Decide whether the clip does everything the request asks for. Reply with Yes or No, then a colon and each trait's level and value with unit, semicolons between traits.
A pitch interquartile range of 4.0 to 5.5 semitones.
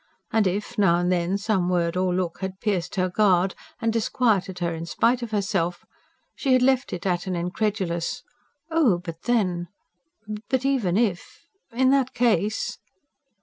Yes: average, 4.6 semitones